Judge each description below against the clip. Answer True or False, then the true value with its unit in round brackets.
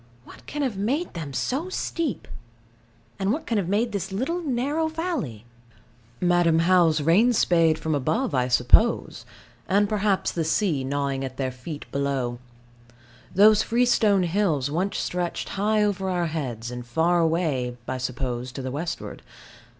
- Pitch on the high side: False (175 Hz)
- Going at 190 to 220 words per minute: False (150 wpm)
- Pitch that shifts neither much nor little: False (7.4 semitones)